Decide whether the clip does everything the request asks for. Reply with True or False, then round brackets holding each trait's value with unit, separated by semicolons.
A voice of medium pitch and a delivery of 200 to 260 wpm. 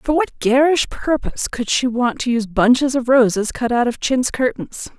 False (250 Hz; 205 wpm)